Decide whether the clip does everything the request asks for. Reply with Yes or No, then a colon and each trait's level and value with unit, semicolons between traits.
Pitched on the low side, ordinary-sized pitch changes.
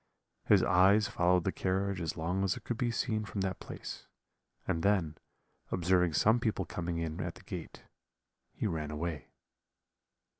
Yes: very low, 90 Hz; average, 3.1 semitones